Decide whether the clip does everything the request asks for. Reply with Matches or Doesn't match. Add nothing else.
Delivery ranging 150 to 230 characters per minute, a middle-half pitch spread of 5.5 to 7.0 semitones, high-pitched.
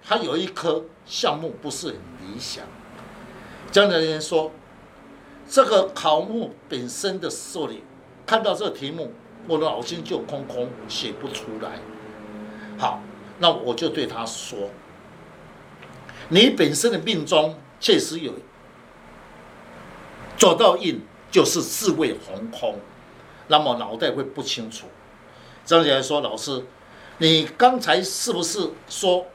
Doesn't match